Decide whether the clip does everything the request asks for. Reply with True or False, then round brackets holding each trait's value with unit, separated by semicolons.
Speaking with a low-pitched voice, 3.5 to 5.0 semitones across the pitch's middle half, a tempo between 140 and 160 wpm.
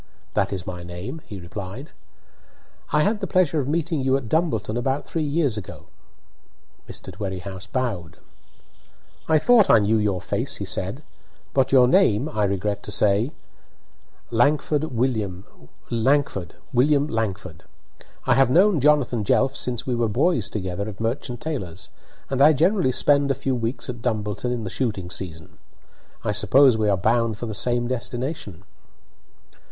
False (120 Hz; 5.6 semitones; 155 wpm)